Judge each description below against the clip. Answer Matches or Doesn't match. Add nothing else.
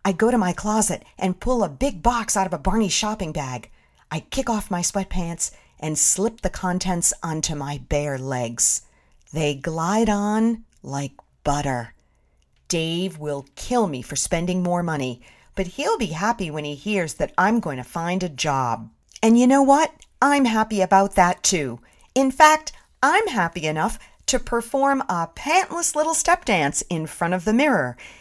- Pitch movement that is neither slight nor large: Doesn't match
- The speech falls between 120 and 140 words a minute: Doesn't match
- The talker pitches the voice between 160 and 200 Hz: Matches